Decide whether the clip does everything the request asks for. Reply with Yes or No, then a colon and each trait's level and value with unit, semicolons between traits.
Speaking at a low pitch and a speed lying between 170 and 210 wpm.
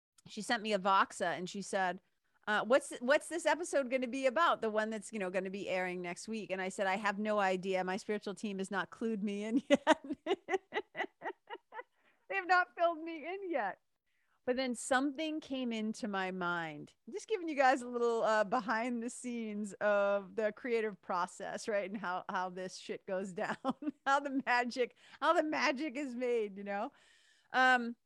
No: high, 230 Hz; average, 195 wpm